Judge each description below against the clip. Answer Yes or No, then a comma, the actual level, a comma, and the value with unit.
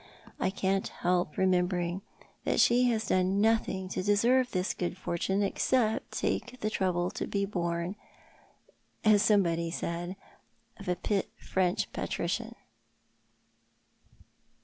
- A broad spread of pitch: No, average, 2.8 semitones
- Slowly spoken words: Yes, slow, 115 wpm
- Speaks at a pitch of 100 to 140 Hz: No, high, 190 Hz